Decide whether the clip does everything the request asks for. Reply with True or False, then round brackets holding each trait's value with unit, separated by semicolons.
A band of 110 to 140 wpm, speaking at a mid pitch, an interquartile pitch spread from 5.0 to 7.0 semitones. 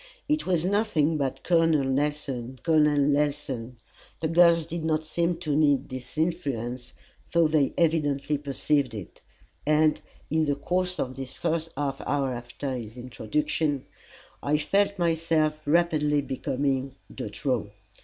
False (135 wpm; 150 Hz; 3.4 semitones)